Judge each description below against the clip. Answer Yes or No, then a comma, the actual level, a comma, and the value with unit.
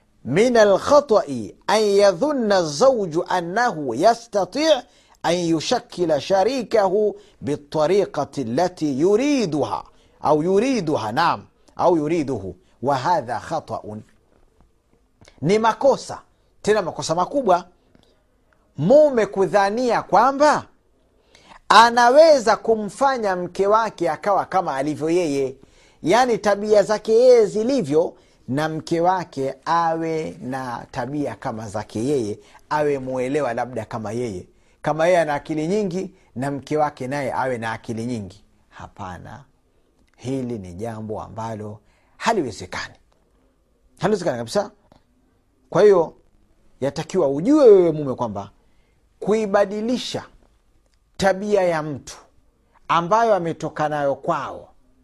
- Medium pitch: Yes, medium, 175 Hz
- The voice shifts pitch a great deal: Yes, wide, 8.0 semitones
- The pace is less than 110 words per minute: Yes, slow, 100 wpm